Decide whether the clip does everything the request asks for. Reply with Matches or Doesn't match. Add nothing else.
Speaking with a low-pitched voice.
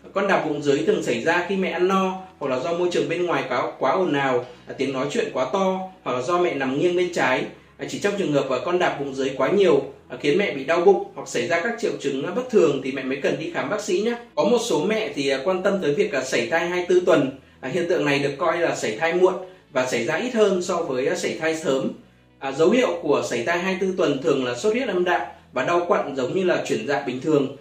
Doesn't match